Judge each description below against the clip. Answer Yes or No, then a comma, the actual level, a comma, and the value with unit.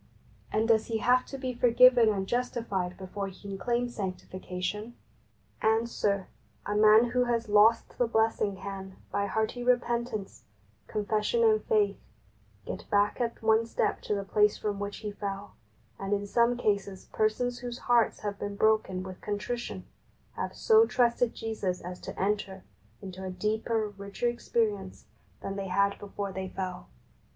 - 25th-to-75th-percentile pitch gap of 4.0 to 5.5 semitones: No, average, 3.2 semitones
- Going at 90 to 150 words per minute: No, average, 160 wpm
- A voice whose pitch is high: Yes, high, 210 Hz